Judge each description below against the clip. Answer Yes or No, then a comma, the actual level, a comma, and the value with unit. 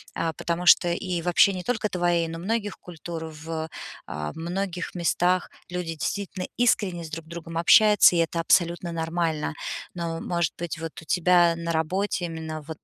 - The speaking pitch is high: No, medium, 170 Hz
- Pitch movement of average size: No, narrow, 1.6 semitones